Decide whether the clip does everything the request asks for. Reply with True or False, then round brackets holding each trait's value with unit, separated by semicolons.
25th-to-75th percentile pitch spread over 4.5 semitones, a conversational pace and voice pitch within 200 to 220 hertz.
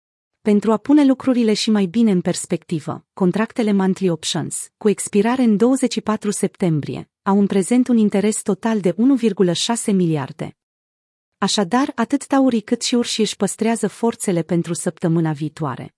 True (4.9 semitones; 140 wpm; 205 Hz)